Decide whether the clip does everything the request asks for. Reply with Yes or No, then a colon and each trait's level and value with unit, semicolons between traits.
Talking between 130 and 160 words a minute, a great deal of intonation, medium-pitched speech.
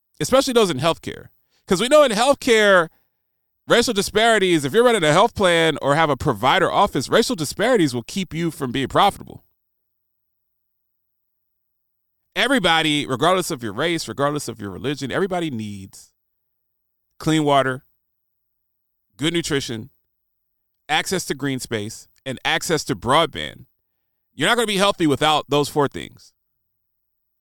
Yes: average, 140 wpm; wide, 7.4 semitones; medium, 150 Hz